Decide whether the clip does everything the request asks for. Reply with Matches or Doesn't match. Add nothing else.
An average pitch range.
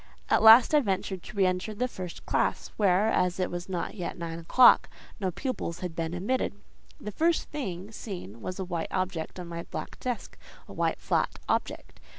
Matches